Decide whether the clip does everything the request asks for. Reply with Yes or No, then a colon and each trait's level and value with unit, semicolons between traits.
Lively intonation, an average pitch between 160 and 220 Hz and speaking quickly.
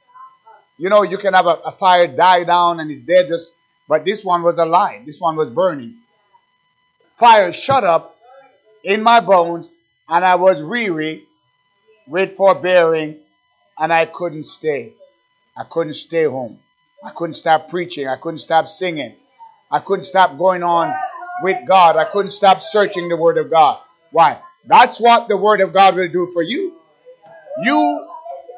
No: wide, 6.3 semitones; medium, 185 Hz; average, 165 wpm